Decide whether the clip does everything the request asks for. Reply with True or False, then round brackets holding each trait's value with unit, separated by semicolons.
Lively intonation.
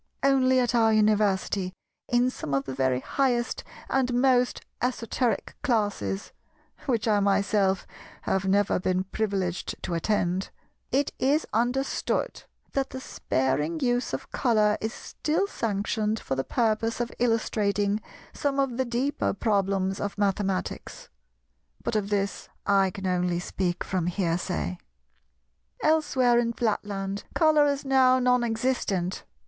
False (4.6 semitones)